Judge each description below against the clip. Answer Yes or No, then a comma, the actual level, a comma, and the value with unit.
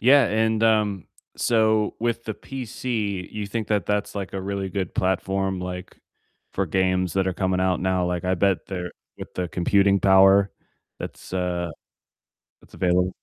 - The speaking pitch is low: Yes, very low, 95 Hz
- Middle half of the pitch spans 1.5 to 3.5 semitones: Yes, narrow, 2.4 semitones